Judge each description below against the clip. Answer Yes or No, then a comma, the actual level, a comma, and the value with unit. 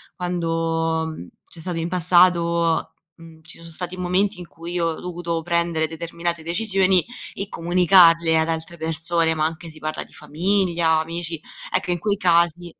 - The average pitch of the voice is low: No, medium, 170 Hz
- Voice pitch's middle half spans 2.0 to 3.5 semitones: No, narrow, 1.5 semitones